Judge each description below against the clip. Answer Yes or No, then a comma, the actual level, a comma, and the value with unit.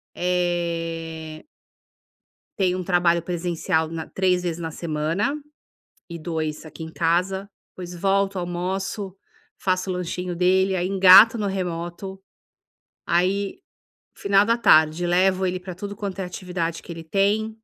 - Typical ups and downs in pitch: No, narrow, 2.2 semitones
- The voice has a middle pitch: Yes, medium, 180 Hz